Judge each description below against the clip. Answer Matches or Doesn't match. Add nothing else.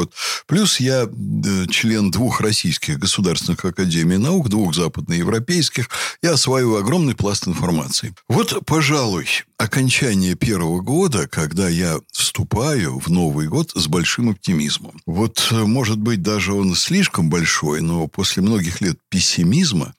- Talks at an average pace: Matches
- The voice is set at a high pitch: Doesn't match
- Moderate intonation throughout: Doesn't match